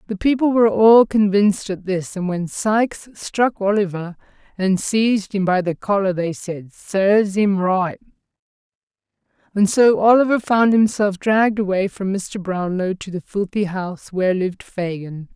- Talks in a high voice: Yes, high, 200 Hz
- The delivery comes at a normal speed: Yes, average, 155 wpm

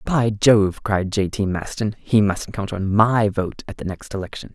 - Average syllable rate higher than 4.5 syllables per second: No, 4.4 syllables/s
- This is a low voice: Yes, low, 105 Hz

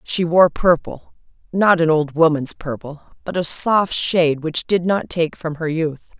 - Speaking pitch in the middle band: Yes, medium, 165 Hz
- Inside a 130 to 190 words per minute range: Yes, average, 185 wpm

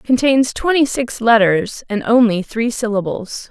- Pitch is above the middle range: Yes, high, 230 Hz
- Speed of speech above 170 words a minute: No, slow, 135 wpm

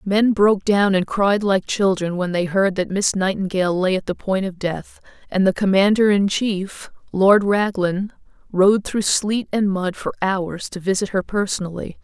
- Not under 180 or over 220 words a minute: Yes, average, 185 wpm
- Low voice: No, high, 195 Hz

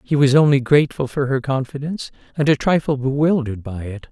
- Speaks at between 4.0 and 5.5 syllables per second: No, 6.1 syllables/s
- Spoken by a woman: No, male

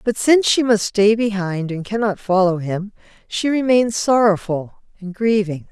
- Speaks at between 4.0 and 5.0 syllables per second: Yes, 4.6 syllables/s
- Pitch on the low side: No, high, 205 Hz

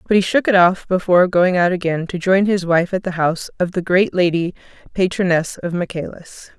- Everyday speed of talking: No, fast, 210 wpm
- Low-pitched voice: No, medium, 180 Hz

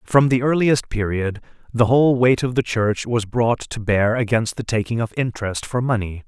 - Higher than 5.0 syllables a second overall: No, 4.9 syllables/s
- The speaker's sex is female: No, male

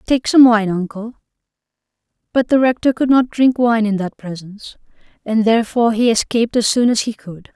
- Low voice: No, high, 225 Hz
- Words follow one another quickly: No, average, 185 wpm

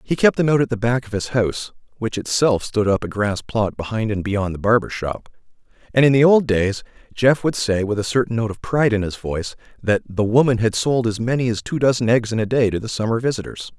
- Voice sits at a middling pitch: No, low, 115 Hz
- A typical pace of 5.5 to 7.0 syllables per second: Yes, 5.8 syllables/s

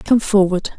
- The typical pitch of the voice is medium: No, high, 200 Hz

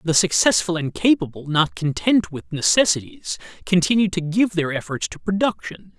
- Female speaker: No, male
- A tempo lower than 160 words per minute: Yes, average, 150 wpm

